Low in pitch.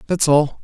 No: medium, 155 Hz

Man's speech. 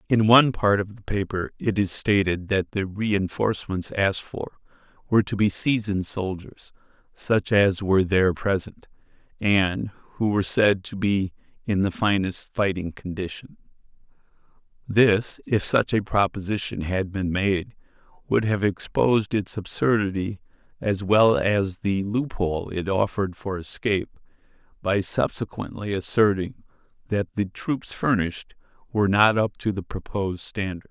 Yes: male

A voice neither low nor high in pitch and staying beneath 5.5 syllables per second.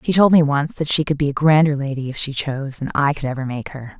No: medium, 145 Hz; 6.3 syllables/s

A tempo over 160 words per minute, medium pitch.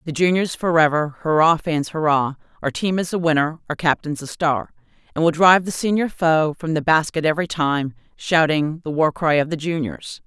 Yes: average, 195 wpm; medium, 160 Hz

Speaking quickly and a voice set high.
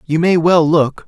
No: fast, 225 wpm; medium, 160 Hz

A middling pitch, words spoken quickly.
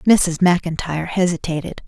No: medium, 170 Hz; slow, 95 wpm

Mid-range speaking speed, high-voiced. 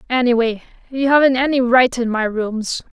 Yes: average, 160 wpm; high, 245 Hz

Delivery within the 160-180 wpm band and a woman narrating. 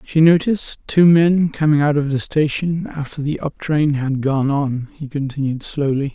No: average, 175 wpm; male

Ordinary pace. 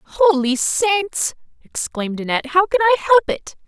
Yes: average, 145 wpm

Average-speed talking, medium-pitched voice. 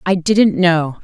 Yes: average, 175 wpm; medium, 175 Hz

